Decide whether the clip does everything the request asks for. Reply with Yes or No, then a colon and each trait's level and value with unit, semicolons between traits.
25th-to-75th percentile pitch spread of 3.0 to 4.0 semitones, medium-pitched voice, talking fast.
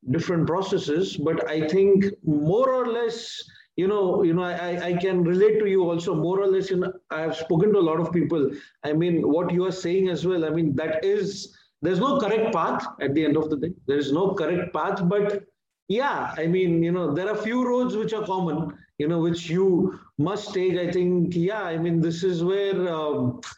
Yes: average, 3.3 semitones; medium, 180 Hz; fast, 220 wpm